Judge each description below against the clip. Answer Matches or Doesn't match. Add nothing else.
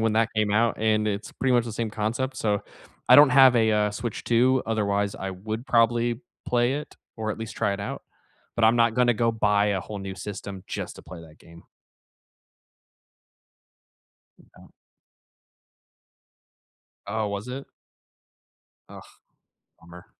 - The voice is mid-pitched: Doesn't match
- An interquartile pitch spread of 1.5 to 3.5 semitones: Matches